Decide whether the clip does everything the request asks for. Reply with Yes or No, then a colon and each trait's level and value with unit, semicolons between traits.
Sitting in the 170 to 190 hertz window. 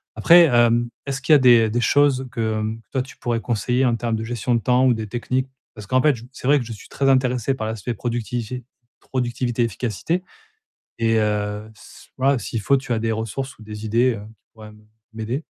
No: low, 120 Hz